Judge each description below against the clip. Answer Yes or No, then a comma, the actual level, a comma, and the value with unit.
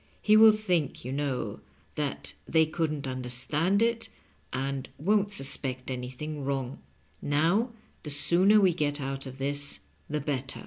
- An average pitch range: Yes, average, 4.7 semitones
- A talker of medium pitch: Yes, medium, 145 Hz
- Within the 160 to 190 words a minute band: No, average, 140 wpm